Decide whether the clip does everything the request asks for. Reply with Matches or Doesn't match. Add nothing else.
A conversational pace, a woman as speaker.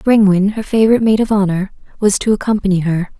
Matches